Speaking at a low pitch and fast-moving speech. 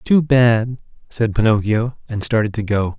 No: low, 115 Hz; average, 160 wpm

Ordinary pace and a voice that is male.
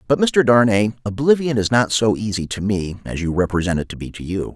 No: fast, 235 wpm; male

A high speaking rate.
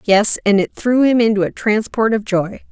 Yes: fast, 220 wpm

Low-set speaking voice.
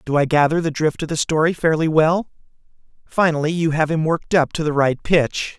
No: medium, 155 Hz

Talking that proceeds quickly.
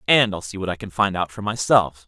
Yes: fast, 290 wpm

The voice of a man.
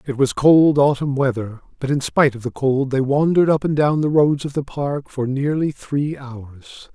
Yes: male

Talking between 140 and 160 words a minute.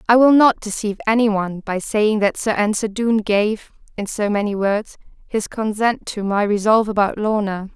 No: average, 185 wpm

